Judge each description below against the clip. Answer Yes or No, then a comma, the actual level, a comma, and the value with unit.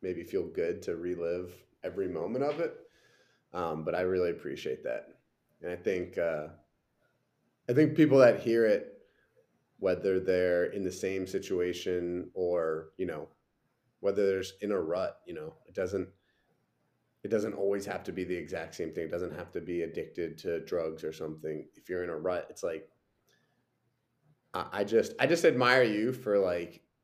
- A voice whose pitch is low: Yes, very low, 95 Hz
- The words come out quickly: No, average, 175 wpm